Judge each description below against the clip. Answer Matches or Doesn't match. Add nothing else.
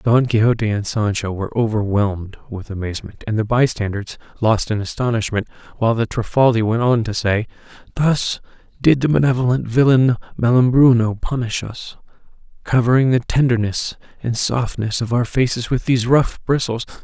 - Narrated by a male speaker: Matches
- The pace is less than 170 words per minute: Matches